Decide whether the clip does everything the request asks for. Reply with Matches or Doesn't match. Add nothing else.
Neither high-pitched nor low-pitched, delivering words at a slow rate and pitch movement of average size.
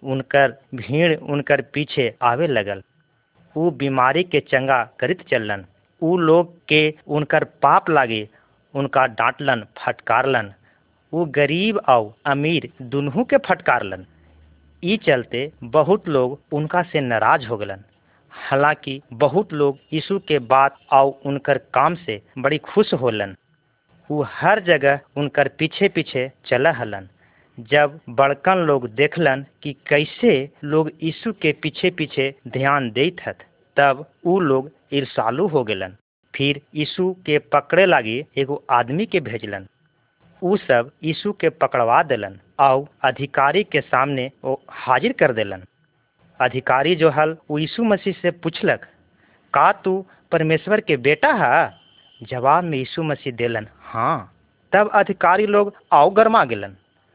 Doesn't match